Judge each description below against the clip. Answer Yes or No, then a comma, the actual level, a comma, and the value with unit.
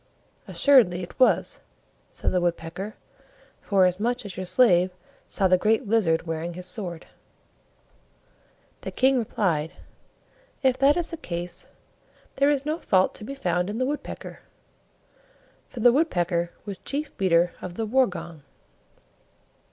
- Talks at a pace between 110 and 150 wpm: Yes, slow, 135 wpm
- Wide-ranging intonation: Yes, wide, 6.4 semitones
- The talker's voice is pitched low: No, high, 195 Hz